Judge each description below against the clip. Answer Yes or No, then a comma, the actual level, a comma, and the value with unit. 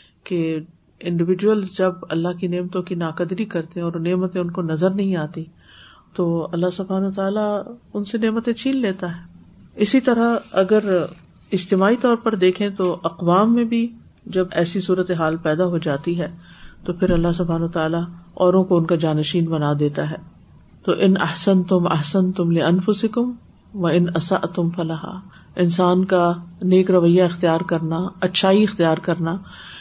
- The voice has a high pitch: No, medium, 180 Hz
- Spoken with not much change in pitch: Yes, narrow, 2.2 semitones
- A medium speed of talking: Yes, average, 160 wpm